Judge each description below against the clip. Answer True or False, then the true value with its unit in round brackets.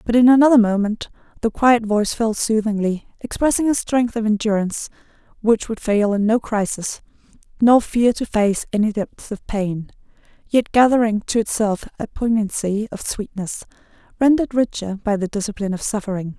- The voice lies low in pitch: False (220 Hz)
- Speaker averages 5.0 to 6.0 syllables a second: True (5.2 syllables/s)